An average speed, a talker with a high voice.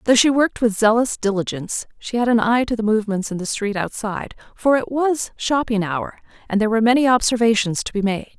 No: fast, 215 wpm; high, 225 Hz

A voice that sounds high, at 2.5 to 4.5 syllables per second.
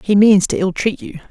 No: high, 195 Hz; 5.3 syllables/s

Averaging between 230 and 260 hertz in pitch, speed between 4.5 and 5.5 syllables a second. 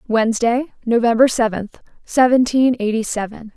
Yes: high, 235 Hz; 5.0 syllables/s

